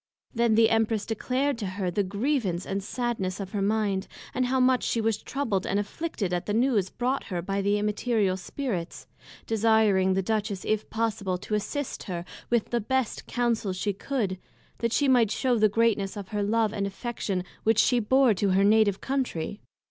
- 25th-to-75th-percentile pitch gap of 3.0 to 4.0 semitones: Yes, average, 3.3 semitones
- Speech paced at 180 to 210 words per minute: Yes, average, 185 wpm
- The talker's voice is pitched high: Yes, high, 215 Hz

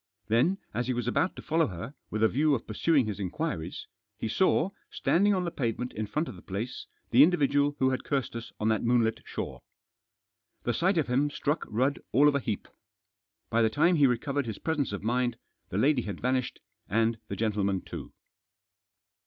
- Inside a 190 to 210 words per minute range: Yes, average, 195 wpm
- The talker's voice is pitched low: Yes, low, 125 Hz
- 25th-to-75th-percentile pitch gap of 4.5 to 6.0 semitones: Yes, average, 4.8 semitones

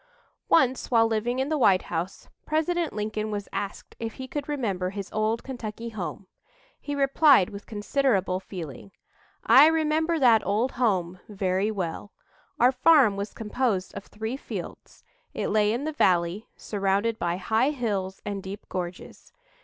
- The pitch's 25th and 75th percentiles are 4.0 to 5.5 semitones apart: Yes, average, 5.2 semitones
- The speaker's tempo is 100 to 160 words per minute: Yes, average, 155 wpm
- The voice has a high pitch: Yes, high, 215 Hz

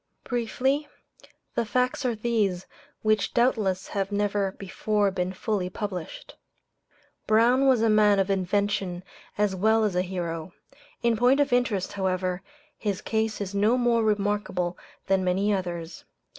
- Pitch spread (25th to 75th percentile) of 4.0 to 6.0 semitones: No, average, 3.1 semitones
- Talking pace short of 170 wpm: Yes, average, 140 wpm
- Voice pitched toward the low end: No, high, 205 Hz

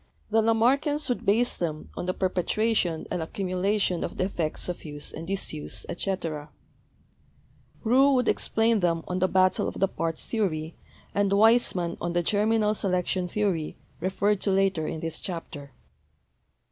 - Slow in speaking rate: No, average, 150 wpm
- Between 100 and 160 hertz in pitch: No, medium, 185 Hz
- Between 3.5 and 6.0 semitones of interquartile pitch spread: Yes, average, 4.1 semitones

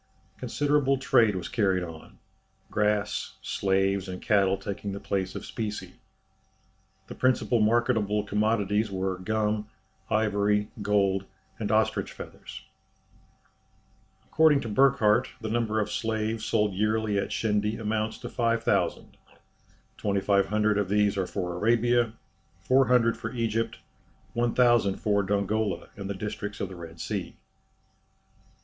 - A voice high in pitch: No, low, 105 Hz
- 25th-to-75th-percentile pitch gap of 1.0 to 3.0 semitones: Yes, narrow, 2.4 semitones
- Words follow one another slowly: Yes, slow, 120 wpm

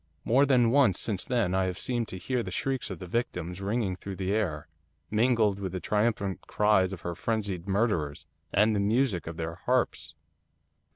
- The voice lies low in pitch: Yes, low, 100 Hz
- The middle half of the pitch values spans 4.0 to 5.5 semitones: Yes, average, 4.3 semitones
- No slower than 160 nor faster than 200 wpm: Yes, average, 185 wpm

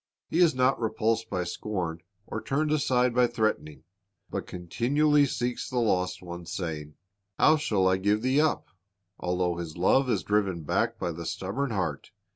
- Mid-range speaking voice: No, low, 105 Hz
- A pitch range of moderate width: No, wide, 6.3 semitones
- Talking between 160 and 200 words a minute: Yes, average, 170 wpm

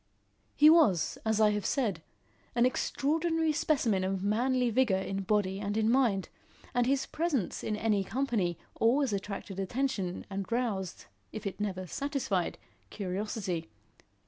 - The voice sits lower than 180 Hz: No, high, 215 Hz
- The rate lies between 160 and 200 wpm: No, average, 140 wpm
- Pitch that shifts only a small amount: No, average, 5.2 semitones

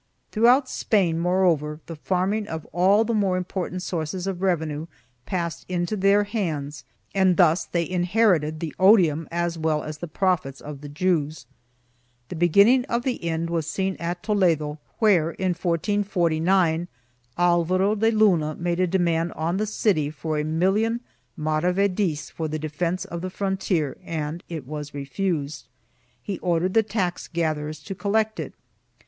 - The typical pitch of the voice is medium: Yes, medium, 175 Hz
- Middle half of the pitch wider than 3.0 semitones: Yes, average, 3.5 semitones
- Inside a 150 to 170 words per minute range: Yes, average, 155 wpm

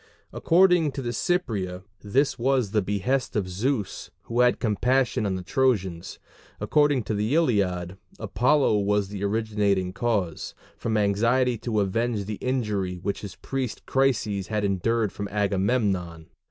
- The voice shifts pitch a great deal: No, average, 4.3 semitones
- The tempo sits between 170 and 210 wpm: No, average, 140 wpm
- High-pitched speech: No, low, 105 Hz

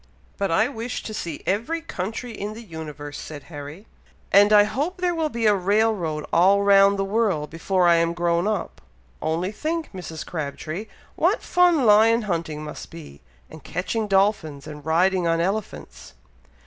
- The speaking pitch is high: Yes, high, 195 Hz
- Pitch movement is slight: No, average, 5.0 semitones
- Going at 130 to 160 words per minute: No, average, 170 wpm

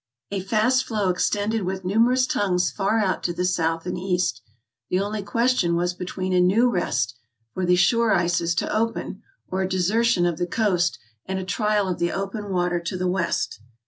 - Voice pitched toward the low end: No, medium, 185 Hz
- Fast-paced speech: No, average, 190 wpm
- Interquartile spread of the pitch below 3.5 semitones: Yes, average, 3.1 semitones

